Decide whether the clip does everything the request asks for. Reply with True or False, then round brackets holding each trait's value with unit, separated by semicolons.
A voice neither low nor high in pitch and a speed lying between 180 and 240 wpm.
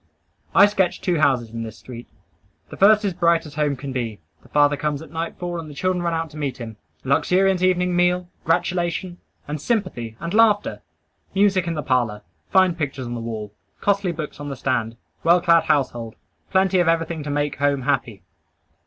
True (160 Hz; 190 wpm)